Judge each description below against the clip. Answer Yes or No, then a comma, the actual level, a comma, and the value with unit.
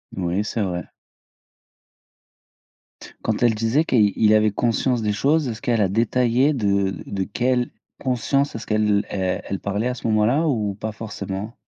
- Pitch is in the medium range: No, low, 110 Hz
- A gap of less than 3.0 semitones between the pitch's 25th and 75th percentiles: No, average, 3.3 semitones